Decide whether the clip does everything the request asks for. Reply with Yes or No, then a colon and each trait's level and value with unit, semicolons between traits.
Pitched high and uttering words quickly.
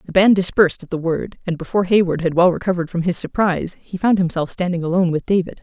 No: medium, 180 Hz; fast, 235 wpm